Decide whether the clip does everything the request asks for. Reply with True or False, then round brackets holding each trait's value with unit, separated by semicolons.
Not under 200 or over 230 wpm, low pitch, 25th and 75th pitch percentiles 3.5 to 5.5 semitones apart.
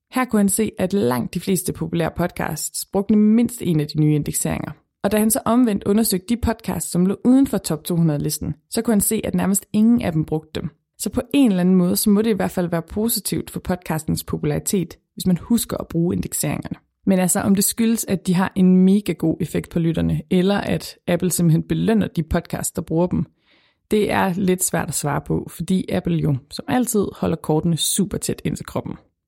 False (220 wpm; 185 Hz; 4.1 semitones)